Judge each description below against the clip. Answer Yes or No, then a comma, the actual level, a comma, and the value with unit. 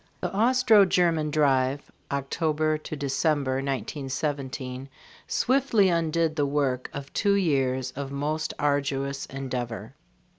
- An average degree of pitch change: Yes, average, 3.0 semitones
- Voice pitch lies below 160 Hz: Yes, medium, 140 Hz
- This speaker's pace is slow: Yes, slow, 105 wpm